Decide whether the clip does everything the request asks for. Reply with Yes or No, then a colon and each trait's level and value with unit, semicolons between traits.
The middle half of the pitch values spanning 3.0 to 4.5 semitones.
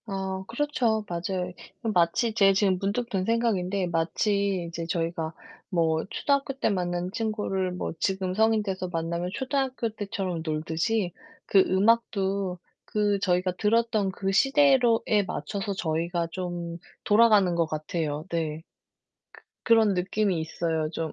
Yes: average, 4.0 semitones